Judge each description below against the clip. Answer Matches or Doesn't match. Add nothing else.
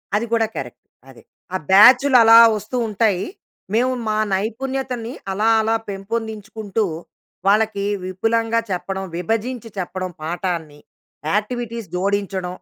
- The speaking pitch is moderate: Doesn't match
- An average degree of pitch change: Matches